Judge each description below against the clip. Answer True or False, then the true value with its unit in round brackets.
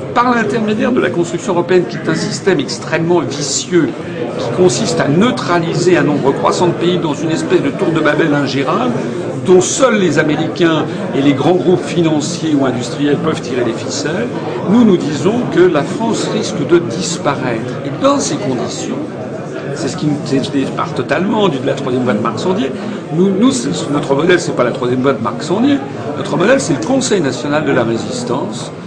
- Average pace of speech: True (185 wpm)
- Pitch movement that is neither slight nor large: True (4.9 semitones)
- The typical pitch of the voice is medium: True (160 Hz)